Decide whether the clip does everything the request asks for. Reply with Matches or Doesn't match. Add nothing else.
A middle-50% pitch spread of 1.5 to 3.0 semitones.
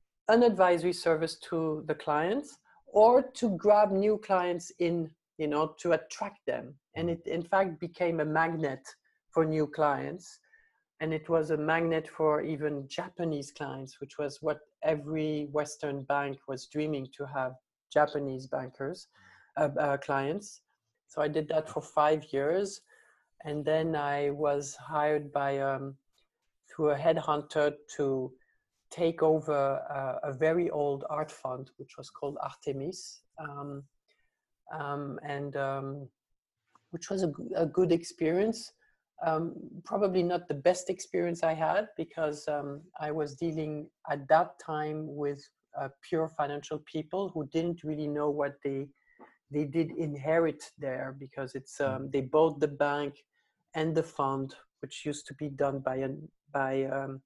Matches